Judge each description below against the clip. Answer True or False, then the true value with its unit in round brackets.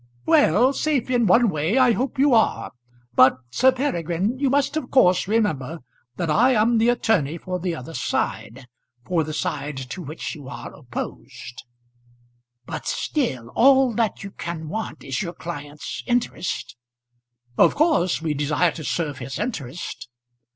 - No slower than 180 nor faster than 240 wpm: False (155 wpm)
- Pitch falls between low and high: True (180 Hz)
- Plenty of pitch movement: True (8.5 semitones)